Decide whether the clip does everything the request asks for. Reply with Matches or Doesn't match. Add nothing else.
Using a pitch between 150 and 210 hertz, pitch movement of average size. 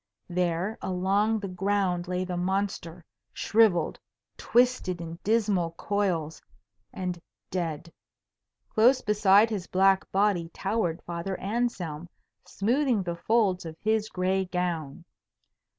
Matches